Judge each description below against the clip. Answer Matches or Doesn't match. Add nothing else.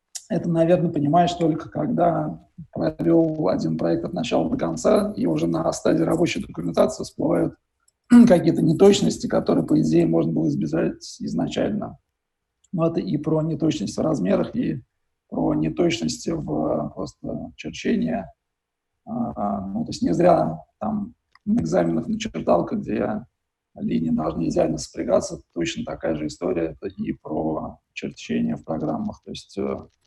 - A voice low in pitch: Doesn't match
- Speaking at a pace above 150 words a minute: Doesn't match